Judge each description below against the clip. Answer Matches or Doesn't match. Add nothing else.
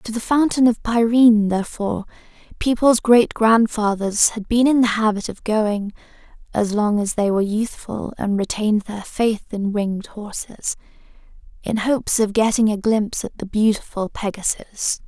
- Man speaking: Doesn't match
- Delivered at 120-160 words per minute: Matches